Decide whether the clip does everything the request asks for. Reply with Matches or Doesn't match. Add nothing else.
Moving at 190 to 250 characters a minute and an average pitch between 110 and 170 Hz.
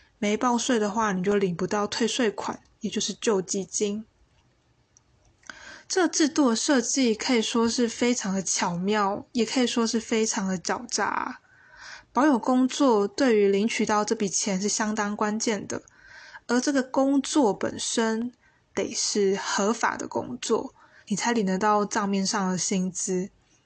Doesn't match